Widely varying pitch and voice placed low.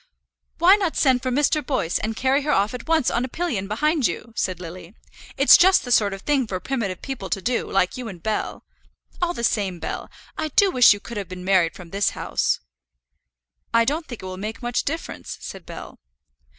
No: wide, 6.4 semitones; high, 235 Hz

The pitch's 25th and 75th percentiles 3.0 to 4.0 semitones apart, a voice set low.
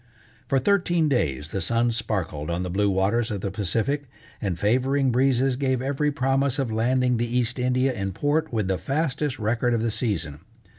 No: average, 4.8 semitones; low, 120 Hz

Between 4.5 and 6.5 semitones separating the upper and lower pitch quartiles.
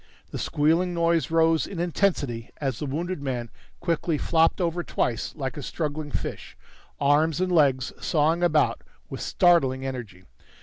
No: average, 4.1 semitones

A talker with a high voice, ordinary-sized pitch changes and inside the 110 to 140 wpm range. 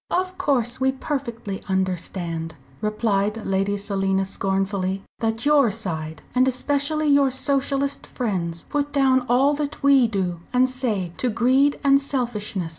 No: high, 235 Hz; wide, 6.1 semitones; slow, 135 wpm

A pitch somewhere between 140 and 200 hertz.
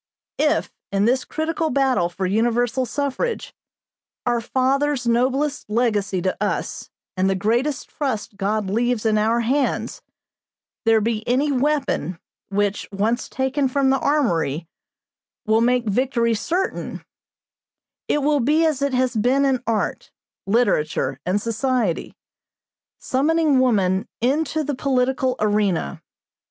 No: high, 245 Hz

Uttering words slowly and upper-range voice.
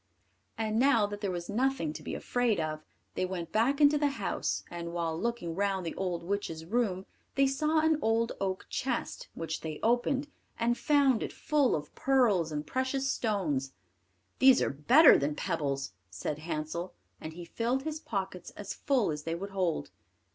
No: average, 175 wpm; high, 200 Hz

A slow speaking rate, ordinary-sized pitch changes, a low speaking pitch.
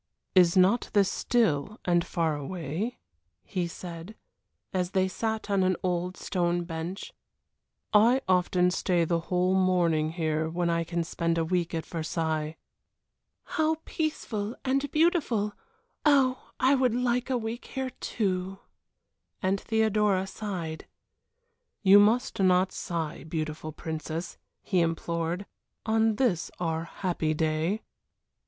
No: slow, 125 wpm; average, 4.6 semitones; medium, 185 Hz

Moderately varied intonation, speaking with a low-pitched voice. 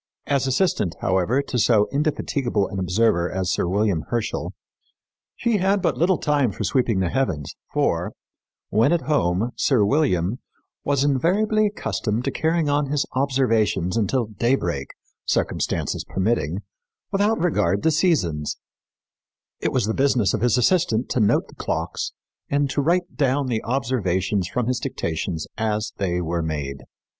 No: wide, 7.0 semitones; low, 120 Hz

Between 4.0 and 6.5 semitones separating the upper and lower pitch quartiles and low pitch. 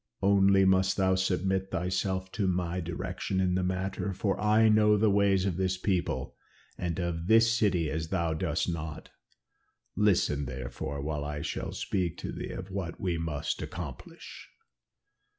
No: narrow, 2.6 semitones; very low, 95 Hz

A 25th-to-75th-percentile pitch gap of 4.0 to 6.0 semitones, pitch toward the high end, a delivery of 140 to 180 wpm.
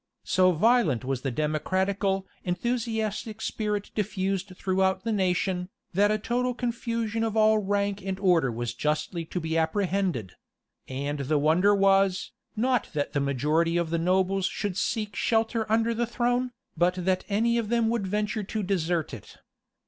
Yes: average, 4.5 semitones; high, 195 Hz; average, 160 wpm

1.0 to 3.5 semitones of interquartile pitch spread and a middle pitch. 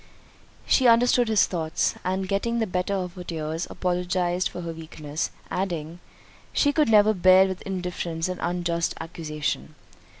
Yes: average, 2.7 semitones; medium, 180 Hz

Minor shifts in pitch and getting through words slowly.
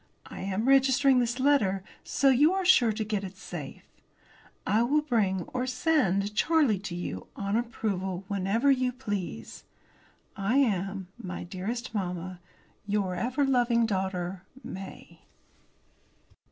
No: average, 5.0 semitones; slow, 130 wpm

